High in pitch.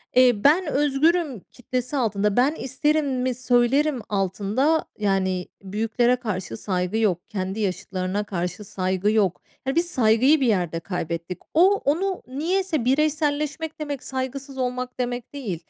Yes: high, 245 Hz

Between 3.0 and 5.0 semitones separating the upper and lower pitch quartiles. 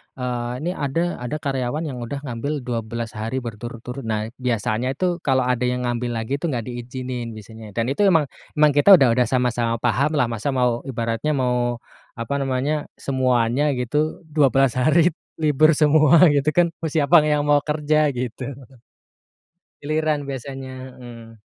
Yes: average, 3.7 semitones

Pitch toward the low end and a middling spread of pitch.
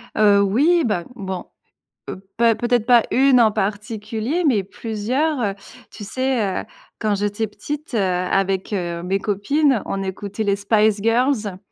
No: high, 215 Hz; average, 3.5 semitones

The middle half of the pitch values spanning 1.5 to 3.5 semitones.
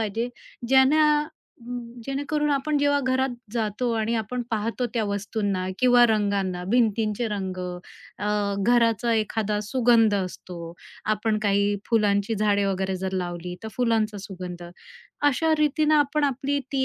No: average, 4.5 semitones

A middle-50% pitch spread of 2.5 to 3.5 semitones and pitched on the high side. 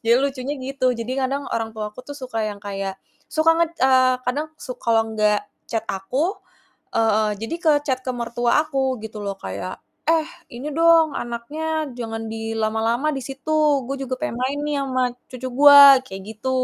No: average, 4.2 semitones; very high, 255 Hz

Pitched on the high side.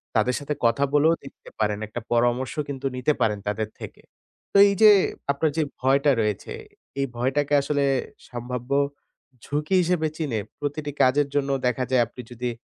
No: low, 135 Hz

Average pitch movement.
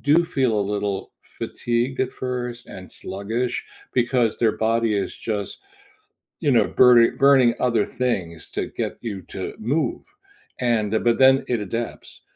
Yes: average, 3.0 semitones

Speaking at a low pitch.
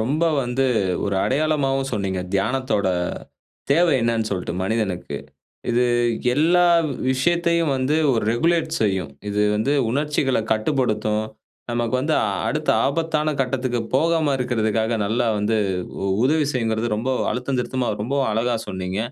Yes: low, 125 Hz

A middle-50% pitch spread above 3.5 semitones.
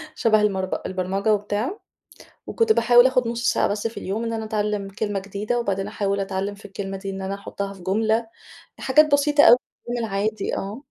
No: average, 2.9 semitones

